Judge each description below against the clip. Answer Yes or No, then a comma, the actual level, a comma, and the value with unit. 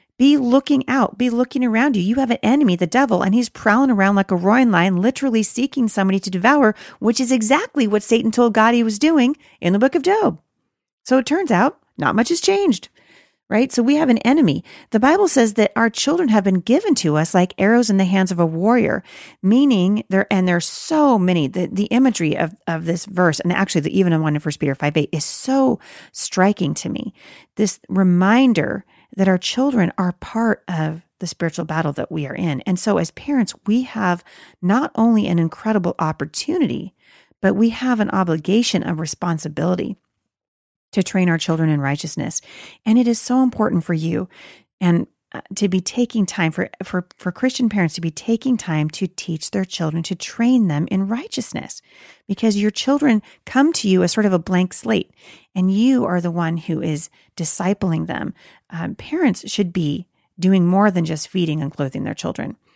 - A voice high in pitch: Yes, high, 200 Hz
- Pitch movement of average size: No, wide, 5.8 semitones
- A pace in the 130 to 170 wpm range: No, average, 195 wpm